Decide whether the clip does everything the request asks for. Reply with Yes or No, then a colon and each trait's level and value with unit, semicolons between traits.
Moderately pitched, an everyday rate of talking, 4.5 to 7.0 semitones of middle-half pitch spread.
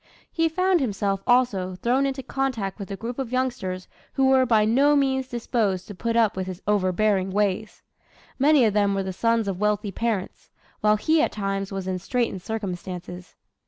No: high, 215 Hz; average, 185 wpm; average, 4.8 semitones